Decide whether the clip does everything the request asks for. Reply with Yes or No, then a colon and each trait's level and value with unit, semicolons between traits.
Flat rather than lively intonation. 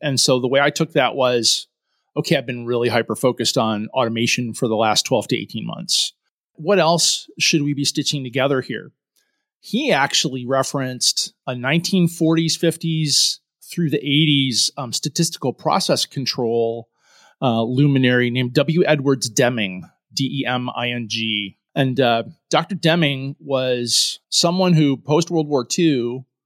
No: average, 4.3 semitones